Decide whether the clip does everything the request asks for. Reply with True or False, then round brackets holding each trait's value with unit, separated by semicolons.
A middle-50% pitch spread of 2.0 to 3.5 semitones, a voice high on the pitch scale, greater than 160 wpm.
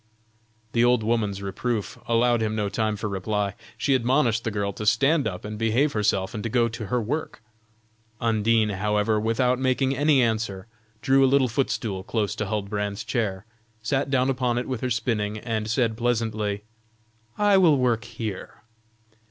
False (3.1 semitones; 115 Hz; 170 wpm)